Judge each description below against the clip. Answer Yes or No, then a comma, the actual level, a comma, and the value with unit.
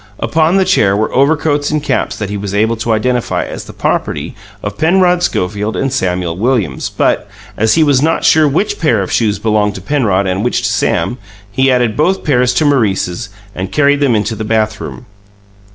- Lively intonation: Yes, wide, 6.0 semitones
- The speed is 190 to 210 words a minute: Yes, average, 195 wpm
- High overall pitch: No, low, 120 Hz